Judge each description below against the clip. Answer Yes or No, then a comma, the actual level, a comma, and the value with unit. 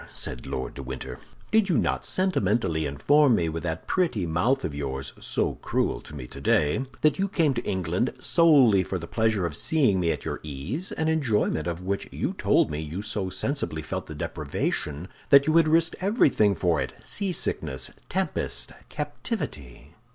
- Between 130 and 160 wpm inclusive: No, average, 175 wpm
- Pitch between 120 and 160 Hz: No, very low, 95 Hz